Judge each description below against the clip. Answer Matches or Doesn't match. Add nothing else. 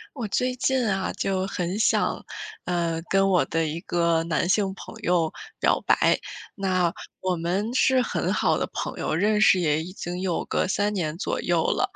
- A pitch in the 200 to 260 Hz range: Doesn't match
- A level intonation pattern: Doesn't match